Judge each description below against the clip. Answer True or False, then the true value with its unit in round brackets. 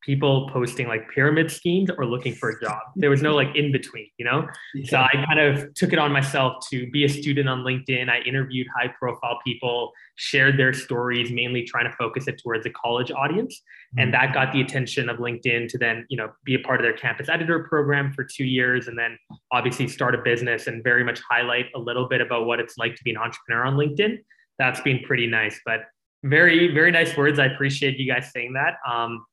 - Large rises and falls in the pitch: False (2.8 semitones)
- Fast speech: True (225 wpm)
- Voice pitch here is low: True (130 Hz)